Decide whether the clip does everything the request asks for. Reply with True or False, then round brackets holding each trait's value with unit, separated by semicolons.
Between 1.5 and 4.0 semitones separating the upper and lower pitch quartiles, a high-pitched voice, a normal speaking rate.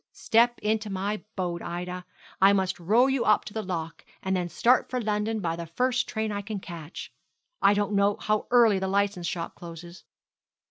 True (3.5 semitones; 200 Hz; 190 wpm)